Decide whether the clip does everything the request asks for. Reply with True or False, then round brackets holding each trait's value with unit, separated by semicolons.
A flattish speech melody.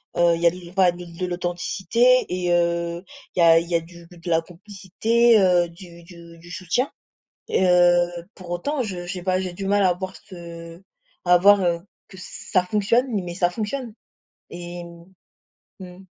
True (1.9 semitones)